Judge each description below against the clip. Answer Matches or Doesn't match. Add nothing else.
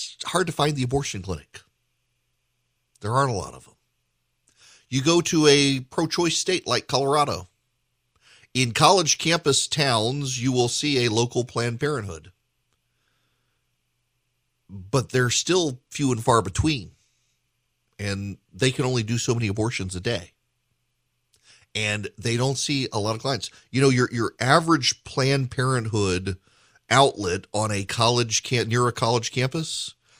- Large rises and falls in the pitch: Doesn't match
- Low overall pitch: Matches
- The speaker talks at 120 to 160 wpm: Matches